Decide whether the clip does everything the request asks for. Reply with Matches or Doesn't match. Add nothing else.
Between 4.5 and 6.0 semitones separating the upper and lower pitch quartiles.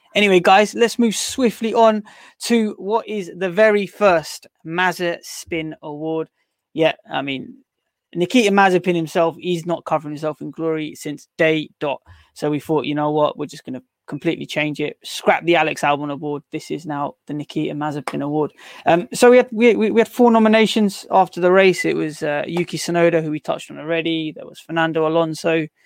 Matches